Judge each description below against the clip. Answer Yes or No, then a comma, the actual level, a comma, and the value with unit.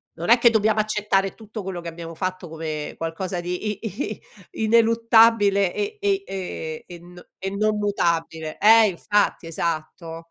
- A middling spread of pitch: Yes, average, 4.5 semitones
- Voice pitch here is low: No, high, 195 Hz